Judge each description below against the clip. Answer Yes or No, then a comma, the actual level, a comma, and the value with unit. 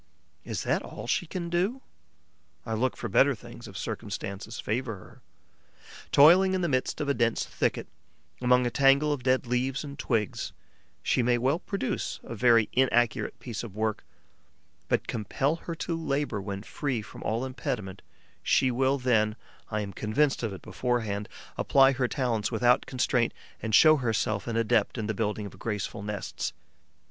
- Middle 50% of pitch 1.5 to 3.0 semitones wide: No, average, 4.0 semitones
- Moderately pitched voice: No, low, 125 Hz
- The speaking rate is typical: Yes, average, 170 wpm